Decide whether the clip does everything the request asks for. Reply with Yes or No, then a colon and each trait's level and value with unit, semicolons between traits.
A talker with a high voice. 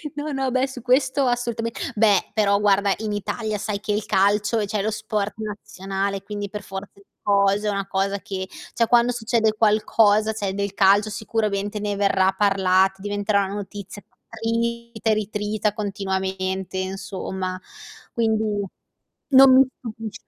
Yes: high, 205 Hz